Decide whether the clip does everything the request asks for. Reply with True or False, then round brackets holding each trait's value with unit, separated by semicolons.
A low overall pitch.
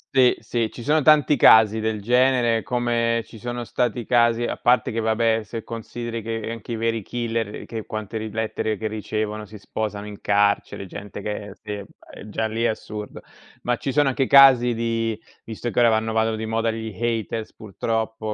True (115 Hz)